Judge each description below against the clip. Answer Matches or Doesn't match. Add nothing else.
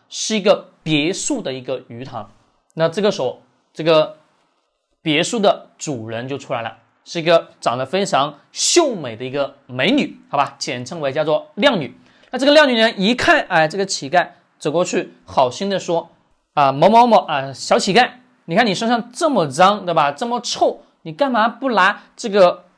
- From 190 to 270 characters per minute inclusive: Matches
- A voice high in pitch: Doesn't match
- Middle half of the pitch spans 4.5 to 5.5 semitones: Doesn't match